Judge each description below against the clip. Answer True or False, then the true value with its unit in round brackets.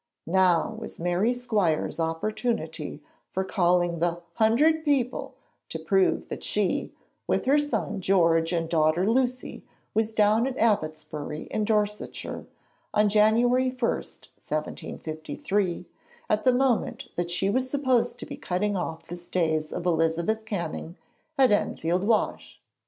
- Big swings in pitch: True (5.7 semitones)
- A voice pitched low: False (205 Hz)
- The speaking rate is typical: False (130 wpm)